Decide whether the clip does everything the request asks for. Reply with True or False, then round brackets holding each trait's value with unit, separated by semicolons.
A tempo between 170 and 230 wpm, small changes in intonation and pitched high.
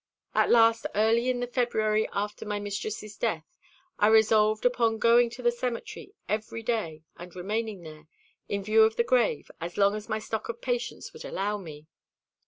True (180 wpm; 2.3 semitones; 220 Hz)